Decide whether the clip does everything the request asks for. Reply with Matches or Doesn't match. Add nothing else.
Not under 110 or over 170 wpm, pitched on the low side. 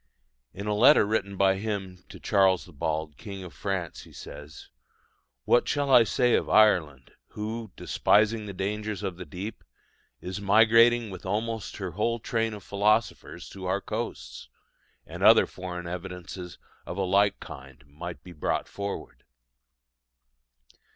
Matches